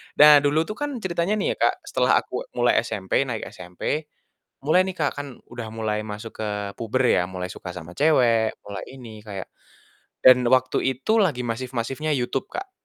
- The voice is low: Yes, low, 125 Hz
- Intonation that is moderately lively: No, wide, 5.9 semitones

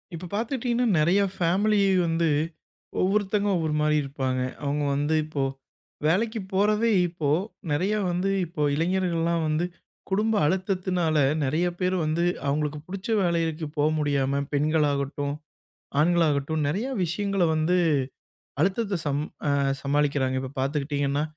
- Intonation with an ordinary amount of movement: Yes, average, 4.5 semitones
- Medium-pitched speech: Yes, medium, 165 Hz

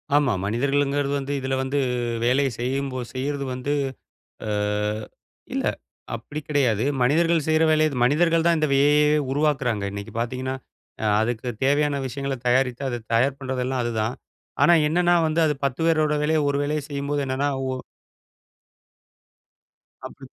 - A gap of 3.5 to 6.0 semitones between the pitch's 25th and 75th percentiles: No, average, 2.9 semitones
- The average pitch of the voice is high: No, medium, 140 Hz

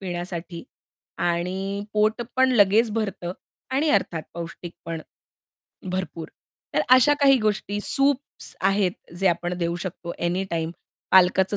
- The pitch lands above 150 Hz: Yes, high, 190 Hz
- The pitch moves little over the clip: No, average, 3.7 semitones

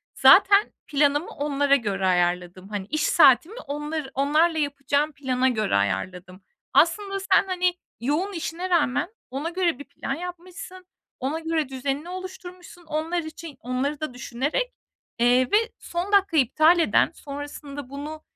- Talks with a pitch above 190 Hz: Yes, very high, 295 Hz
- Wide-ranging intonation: No, average, 4.9 semitones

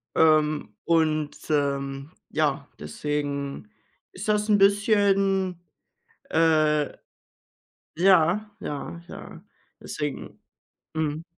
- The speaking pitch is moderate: Yes, medium, 160 Hz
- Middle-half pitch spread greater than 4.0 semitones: Yes, average, 4.7 semitones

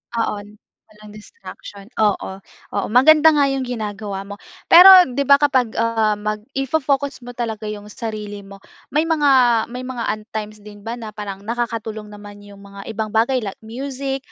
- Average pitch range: Yes, average, 3.8 semitones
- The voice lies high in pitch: Yes, high, 220 Hz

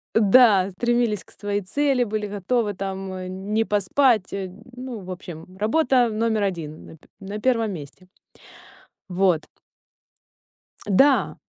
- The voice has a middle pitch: No, high, 205 Hz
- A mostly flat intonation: No, average, 4.1 semitones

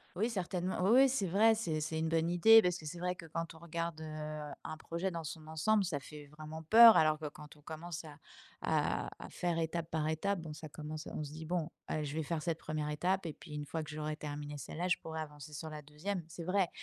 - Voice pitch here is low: No, medium, 160 Hz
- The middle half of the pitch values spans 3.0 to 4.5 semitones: No, narrow, 2.5 semitones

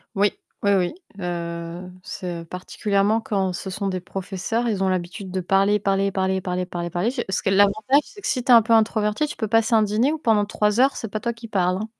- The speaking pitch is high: Yes, high, 200 Hz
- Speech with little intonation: No, average, 3.0 semitones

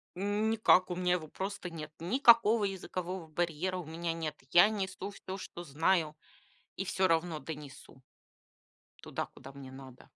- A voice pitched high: No, medium, 175 Hz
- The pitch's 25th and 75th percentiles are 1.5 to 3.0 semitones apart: No, average, 3.5 semitones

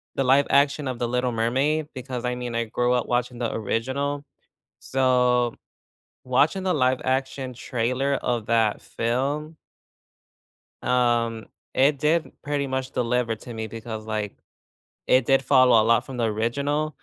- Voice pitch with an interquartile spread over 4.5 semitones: No, average, 2.7 semitones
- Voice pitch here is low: Yes, low, 125 Hz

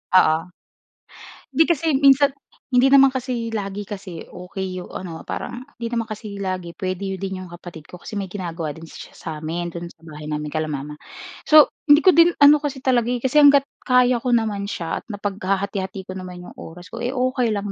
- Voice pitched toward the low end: No, high, 200 Hz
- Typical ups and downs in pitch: No, wide, 6.2 semitones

